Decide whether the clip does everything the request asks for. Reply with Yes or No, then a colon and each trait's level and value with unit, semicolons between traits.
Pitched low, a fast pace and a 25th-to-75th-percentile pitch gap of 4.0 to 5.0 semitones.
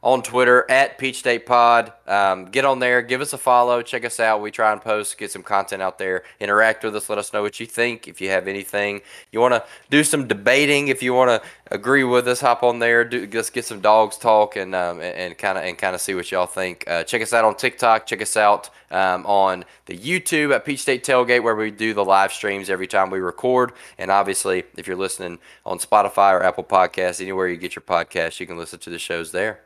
Yes: low, 110 Hz; fast, 245 wpm; average, 4.4 semitones